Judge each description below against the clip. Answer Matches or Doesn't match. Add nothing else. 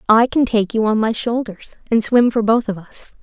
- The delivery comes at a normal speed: Doesn't match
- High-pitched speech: Matches